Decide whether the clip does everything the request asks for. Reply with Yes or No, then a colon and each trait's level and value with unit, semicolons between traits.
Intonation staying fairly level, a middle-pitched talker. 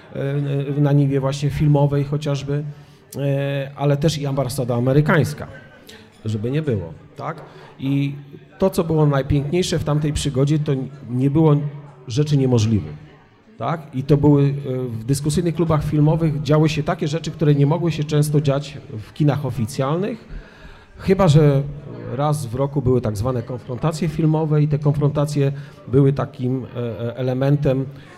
Yes: narrow, 2.0 semitones; medium, 145 Hz